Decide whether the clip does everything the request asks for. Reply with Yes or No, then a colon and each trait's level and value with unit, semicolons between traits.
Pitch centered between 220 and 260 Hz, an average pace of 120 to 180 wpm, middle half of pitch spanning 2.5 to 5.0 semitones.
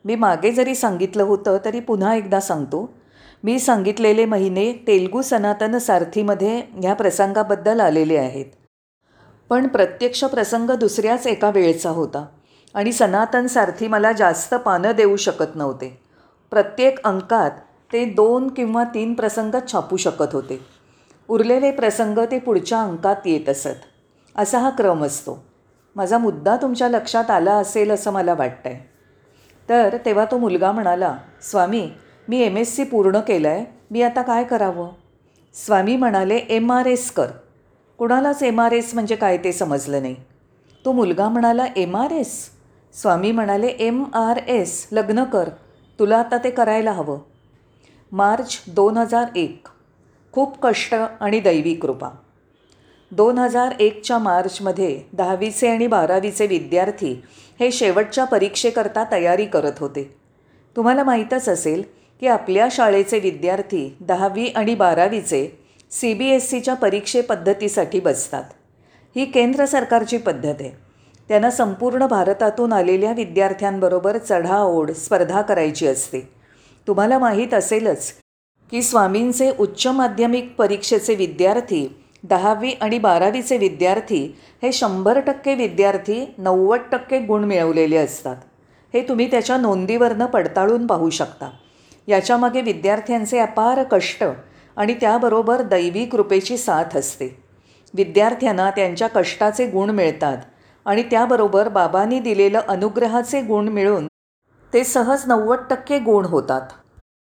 No: high, 210 Hz; average, 125 wpm; average, 4.4 semitones